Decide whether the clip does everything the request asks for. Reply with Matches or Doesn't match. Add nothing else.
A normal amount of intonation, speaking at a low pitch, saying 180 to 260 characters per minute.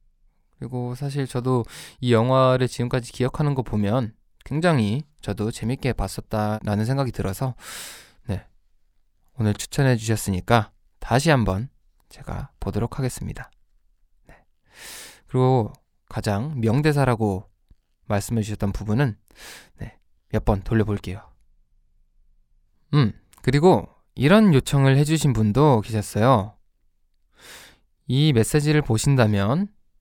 Matches